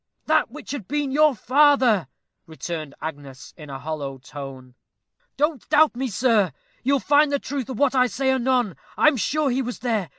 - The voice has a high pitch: Yes, very high, 250 Hz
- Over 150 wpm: Yes, average, 185 wpm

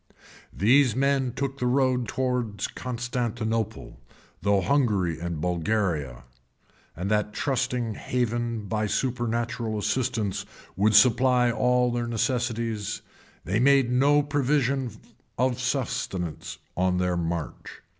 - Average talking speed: No, slow, 110 wpm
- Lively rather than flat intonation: No, average, 3.7 semitones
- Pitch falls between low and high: No, low, 120 Hz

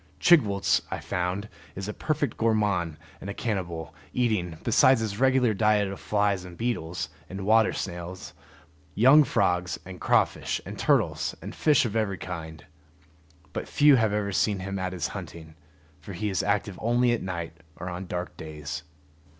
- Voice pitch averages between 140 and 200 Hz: No, low, 100 Hz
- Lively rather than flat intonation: No, average, 4.0 semitones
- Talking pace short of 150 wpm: No, average, 165 wpm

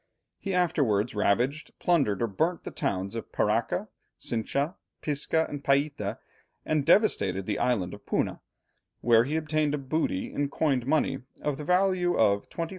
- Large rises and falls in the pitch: Yes, wide, 6.4 semitones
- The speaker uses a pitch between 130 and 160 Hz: Yes, medium, 140 Hz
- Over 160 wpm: No, average, 155 wpm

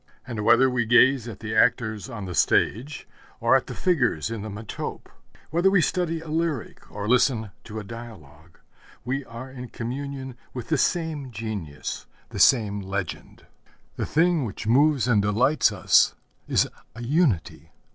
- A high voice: No, low, 120 Hz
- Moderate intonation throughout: Yes, average, 4.6 semitones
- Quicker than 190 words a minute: No, average, 160 wpm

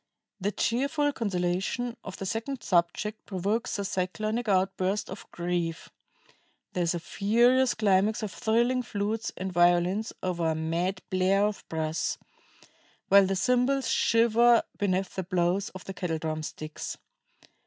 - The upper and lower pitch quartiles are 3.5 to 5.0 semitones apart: Yes, average, 4.0 semitones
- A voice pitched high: Yes, high, 195 Hz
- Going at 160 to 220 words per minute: No, average, 145 wpm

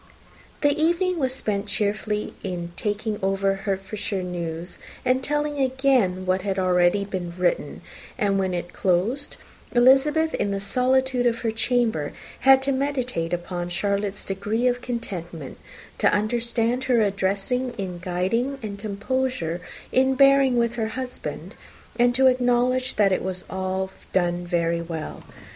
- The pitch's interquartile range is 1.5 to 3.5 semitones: No, average, 5.3 semitones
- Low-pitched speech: No, high, 210 Hz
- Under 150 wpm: Yes, average, 140 wpm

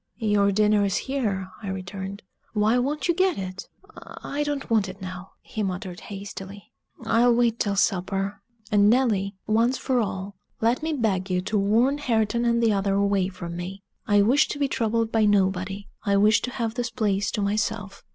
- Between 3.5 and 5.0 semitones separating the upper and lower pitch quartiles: No, average, 3.1 semitones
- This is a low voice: No, high, 205 Hz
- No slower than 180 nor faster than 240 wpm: Yes, average, 185 wpm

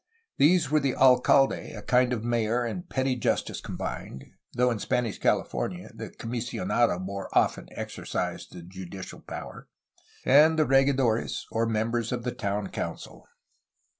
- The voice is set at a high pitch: No, low, 120 Hz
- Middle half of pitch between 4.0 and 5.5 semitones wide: No, average, 3.6 semitones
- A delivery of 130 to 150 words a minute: Yes, average, 140 wpm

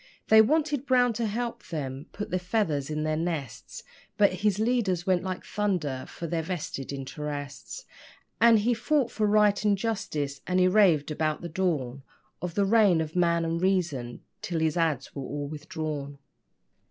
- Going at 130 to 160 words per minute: No, average, 170 wpm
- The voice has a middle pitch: Yes, medium, 175 Hz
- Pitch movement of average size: No, wide, 5.7 semitones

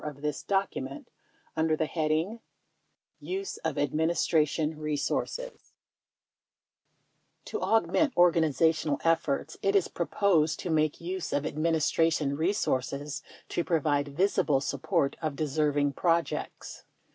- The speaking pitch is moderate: Yes, medium, 155 Hz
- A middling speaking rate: No, slow, 115 wpm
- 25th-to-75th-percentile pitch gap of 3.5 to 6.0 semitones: No, average, 2.8 semitones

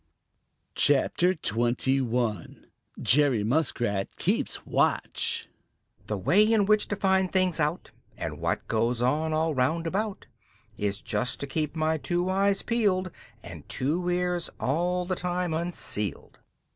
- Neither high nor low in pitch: Yes, medium, 160 Hz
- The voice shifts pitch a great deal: Yes, wide, 6.4 semitones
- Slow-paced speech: Yes, slow, 130 wpm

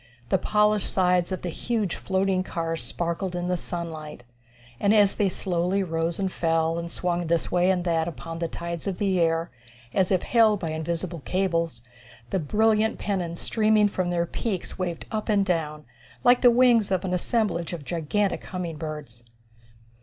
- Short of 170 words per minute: No, average, 175 wpm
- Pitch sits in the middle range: Yes, medium, 180 Hz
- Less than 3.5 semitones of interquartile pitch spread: Yes, average, 3.1 semitones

